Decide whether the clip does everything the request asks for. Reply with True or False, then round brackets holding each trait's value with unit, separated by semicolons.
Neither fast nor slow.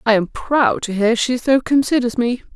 False (210 wpm)